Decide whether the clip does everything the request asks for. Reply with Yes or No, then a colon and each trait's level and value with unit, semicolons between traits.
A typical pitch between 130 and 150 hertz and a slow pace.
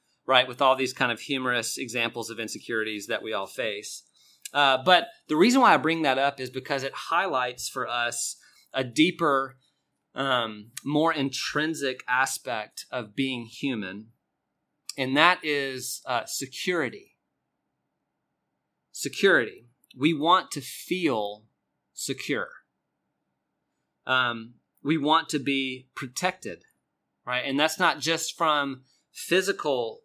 Yes: low, 135 Hz; slow, 125 wpm